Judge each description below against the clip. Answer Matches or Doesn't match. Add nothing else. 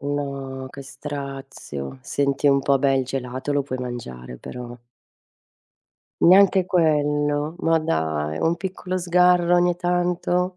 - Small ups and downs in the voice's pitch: Doesn't match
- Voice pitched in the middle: Matches